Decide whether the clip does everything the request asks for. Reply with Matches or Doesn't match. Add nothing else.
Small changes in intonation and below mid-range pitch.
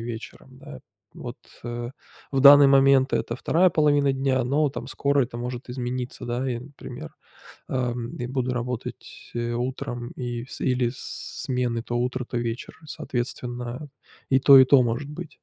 Matches